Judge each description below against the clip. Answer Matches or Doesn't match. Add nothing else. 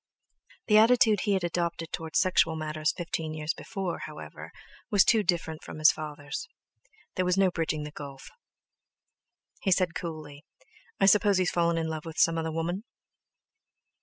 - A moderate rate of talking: Matches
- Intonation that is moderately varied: Matches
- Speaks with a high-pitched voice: Doesn't match